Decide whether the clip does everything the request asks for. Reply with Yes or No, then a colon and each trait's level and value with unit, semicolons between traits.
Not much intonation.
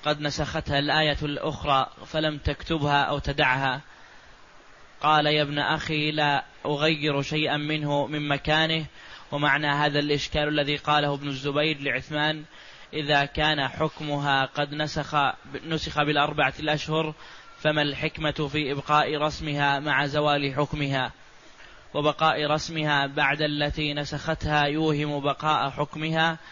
Yes: narrow, 1.1 semitones